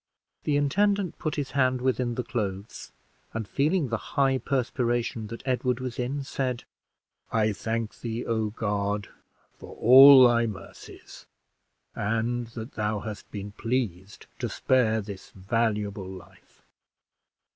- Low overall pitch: Yes, low, 115 Hz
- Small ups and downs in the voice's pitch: No, average, 3.5 semitones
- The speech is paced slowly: Yes, slow, 130 wpm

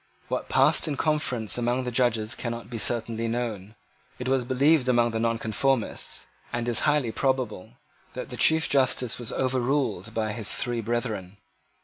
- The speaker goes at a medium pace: Yes, average, 155 wpm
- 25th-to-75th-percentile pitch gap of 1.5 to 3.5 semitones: Yes, narrow, 2.5 semitones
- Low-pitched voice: Yes, low, 120 Hz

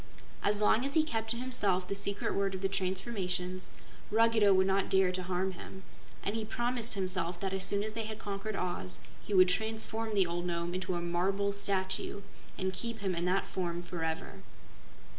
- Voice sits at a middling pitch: No, high, 195 Hz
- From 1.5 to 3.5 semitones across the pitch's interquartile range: Yes, average, 2.9 semitones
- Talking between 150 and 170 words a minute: No, average, 195 wpm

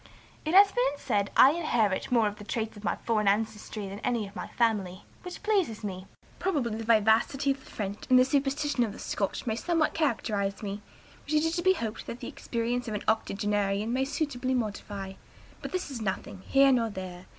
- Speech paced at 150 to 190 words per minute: No, fast, 205 wpm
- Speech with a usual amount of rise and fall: Yes, average, 4.8 semitones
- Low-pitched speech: No, high, 230 Hz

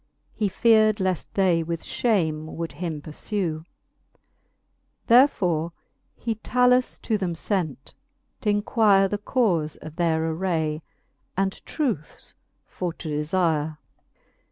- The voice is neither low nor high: Yes, medium, 180 Hz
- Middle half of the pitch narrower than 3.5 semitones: No, average, 4.7 semitones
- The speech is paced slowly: Yes, slow, 105 wpm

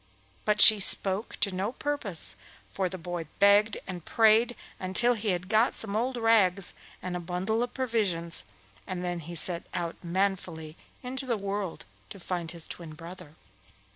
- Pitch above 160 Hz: Yes, high, 190 Hz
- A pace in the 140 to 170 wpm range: Yes, average, 165 wpm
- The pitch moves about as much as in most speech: Yes, average, 3.8 semitones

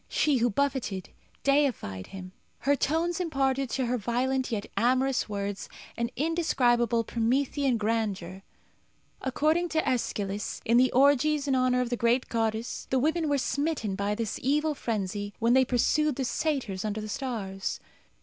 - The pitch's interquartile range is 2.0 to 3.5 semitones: No, average, 4.4 semitones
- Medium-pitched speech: No, very high, 250 Hz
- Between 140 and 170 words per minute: Yes, average, 150 wpm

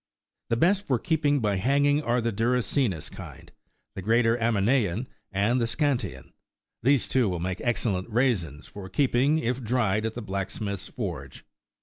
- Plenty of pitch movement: No, average, 4.6 semitones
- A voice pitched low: Yes, low, 115 Hz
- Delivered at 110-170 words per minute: Yes, average, 160 wpm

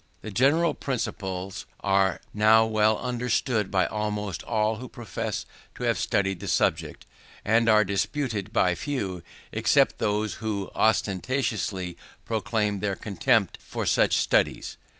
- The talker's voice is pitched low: Yes, low, 105 Hz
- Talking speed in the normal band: No, slow, 130 wpm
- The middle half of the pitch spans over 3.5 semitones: No, average, 2.9 semitones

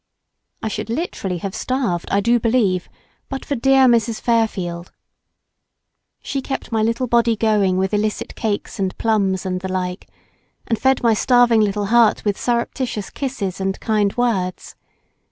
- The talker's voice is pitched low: No, high, 220 Hz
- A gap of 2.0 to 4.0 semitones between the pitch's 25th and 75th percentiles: Yes, average, 3.7 semitones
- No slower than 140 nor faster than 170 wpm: Yes, average, 155 wpm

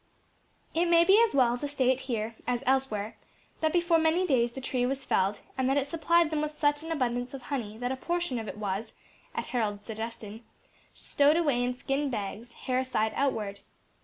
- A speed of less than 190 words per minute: No, average, 195 wpm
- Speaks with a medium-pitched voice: No, very high, 260 Hz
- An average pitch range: Yes, average, 4.5 semitones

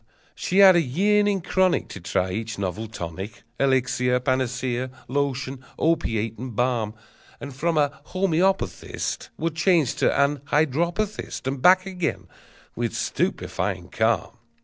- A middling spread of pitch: No, wide, 6.5 semitones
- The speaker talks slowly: Yes, slow, 125 wpm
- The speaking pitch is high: No, low, 135 Hz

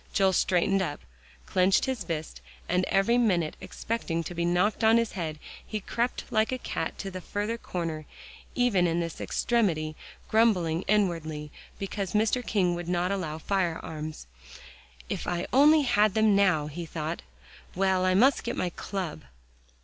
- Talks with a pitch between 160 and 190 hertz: Yes, medium, 185 Hz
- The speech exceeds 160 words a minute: No, average, 155 wpm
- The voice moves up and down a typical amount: Yes, average, 4.3 semitones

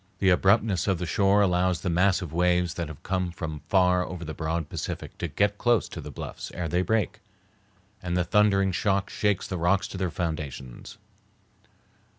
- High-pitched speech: No, very low, 90 Hz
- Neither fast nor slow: Yes, average, 180 wpm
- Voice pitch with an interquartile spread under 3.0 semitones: Yes, narrow, 2.4 semitones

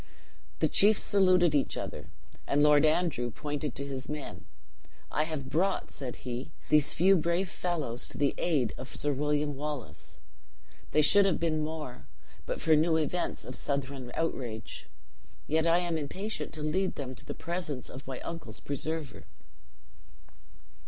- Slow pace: No, average, 155 wpm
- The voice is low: No, medium, 150 Hz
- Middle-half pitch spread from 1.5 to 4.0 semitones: Yes, average, 3.5 semitones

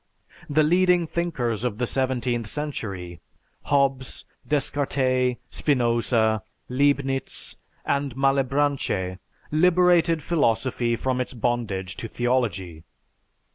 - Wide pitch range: No, average, 3.7 semitones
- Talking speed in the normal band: No, slow, 90 wpm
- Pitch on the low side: Yes, low, 130 Hz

